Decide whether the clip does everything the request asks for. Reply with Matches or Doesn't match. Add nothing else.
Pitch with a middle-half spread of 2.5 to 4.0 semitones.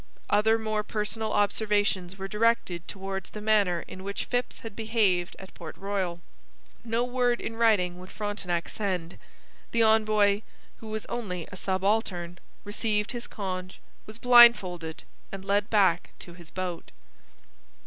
Matches